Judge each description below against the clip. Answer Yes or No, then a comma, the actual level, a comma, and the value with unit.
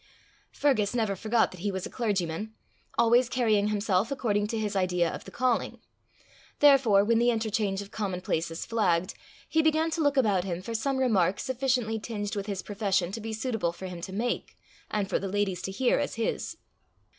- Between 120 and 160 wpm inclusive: No, average, 190 wpm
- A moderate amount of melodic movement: Yes, average, 3.6 semitones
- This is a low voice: No, high, 215 Hz